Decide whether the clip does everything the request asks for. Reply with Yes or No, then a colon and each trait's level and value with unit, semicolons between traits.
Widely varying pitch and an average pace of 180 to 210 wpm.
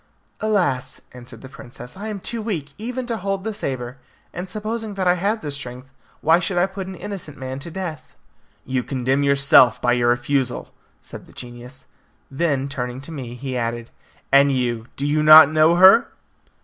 Yes: wide, 6.7 semitones; average, 185 wpm